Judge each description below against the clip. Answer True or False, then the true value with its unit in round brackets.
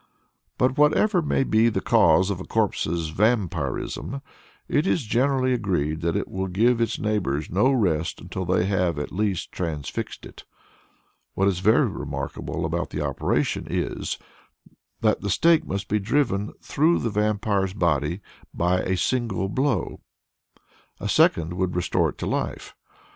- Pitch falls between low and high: False (100 Hz)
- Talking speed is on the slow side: False (150 wpm)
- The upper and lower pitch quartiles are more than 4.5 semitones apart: True (5.0 semitones)